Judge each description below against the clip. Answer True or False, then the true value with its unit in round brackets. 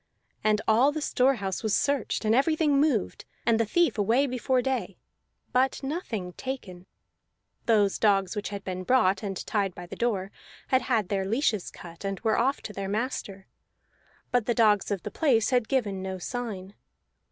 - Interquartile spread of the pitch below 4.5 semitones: False (4.8 semitones)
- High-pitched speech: True (220 Hz)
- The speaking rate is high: False (175 wpm)